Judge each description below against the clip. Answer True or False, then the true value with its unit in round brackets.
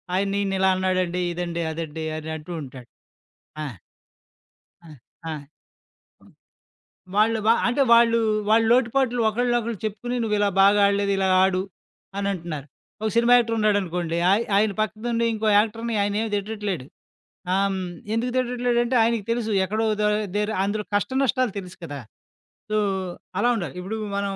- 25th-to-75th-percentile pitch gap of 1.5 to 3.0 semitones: False (3.7 semitones)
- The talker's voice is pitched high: True (210 Hz)